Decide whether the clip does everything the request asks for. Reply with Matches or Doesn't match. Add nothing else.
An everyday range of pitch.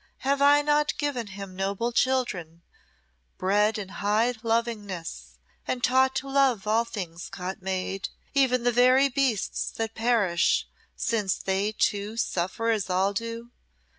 Matches